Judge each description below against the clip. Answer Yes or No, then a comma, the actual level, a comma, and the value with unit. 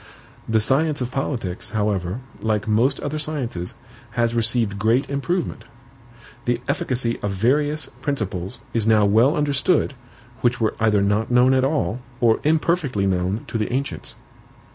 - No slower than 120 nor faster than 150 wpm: Yes, average, 140 wpm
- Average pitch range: Yes, average, 4.6 semitones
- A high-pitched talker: No, low, 120 Hz